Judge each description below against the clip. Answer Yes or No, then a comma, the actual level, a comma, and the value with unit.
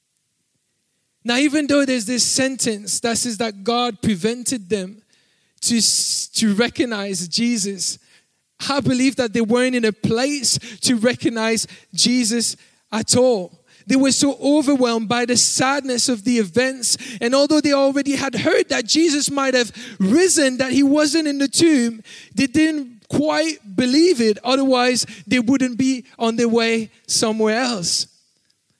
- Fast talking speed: No, average, 145 wpm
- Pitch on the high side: Yes, high, 245 Hz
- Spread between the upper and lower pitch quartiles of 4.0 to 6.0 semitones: No, average, 3.3 semitones